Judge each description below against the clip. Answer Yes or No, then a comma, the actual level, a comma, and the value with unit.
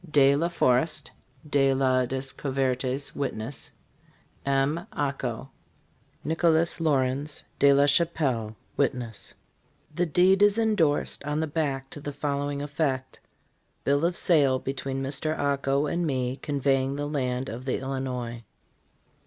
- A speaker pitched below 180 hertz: Yes, medium, 140 Hz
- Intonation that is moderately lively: No, narrow, 2.3 semitones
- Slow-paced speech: Yes, slow, 130 wpm